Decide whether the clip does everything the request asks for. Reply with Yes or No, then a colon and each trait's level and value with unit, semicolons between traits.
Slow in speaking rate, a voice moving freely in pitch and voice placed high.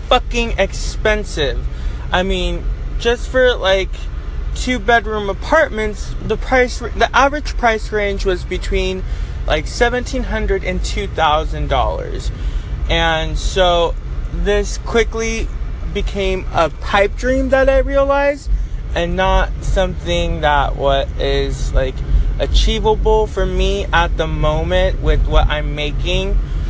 Yes: slow, 110 wpm; wide, 7.9 semitones; high, 195 Hz